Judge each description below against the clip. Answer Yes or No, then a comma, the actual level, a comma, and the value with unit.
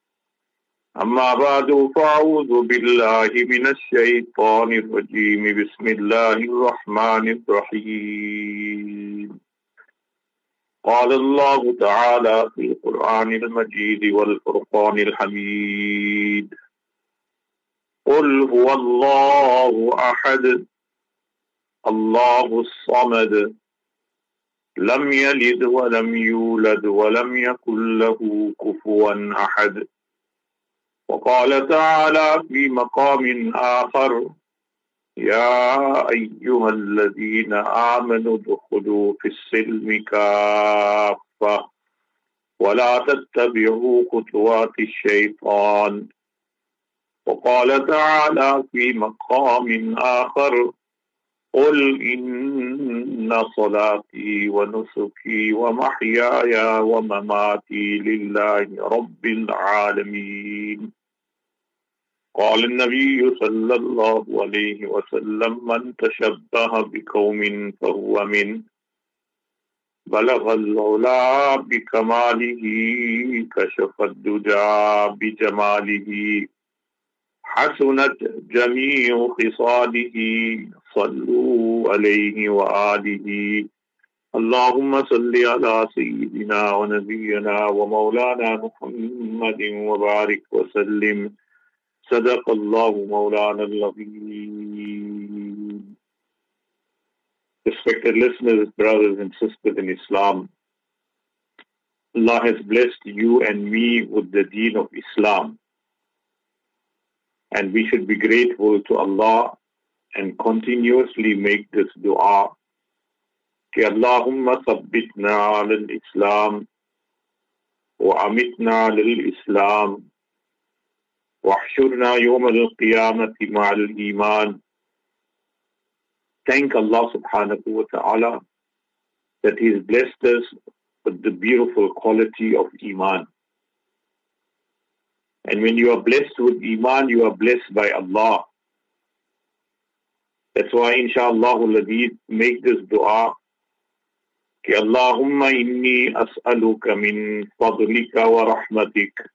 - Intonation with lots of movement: Yes, wide, 6.6 semitones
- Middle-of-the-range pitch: No, low, 120 Hz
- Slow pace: Yes, slow, 75 wpm